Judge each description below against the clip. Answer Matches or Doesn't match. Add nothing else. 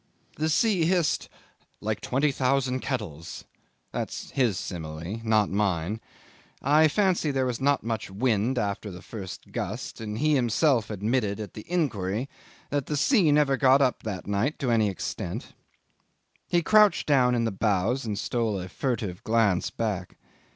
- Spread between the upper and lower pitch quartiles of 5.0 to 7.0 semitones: Matches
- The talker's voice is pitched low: Matches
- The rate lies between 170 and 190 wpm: Doesn't match